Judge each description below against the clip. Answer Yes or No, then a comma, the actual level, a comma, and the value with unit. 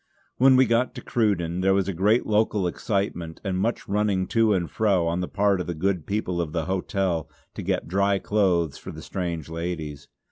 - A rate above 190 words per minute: Yes, average, 200 wpm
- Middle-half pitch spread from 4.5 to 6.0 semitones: No, average, 3.4 semitones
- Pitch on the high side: No, very low, 95 Hz